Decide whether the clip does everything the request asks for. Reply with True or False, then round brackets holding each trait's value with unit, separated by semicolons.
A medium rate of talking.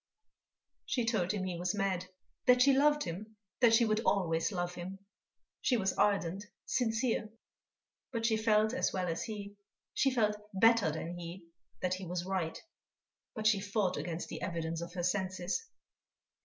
True (165 wpm)